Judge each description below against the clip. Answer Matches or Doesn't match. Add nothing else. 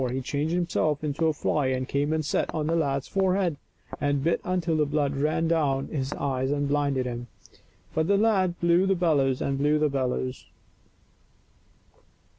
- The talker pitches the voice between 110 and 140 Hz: Doesn't match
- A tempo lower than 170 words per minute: Doesn't match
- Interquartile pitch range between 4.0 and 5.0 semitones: Doesn't match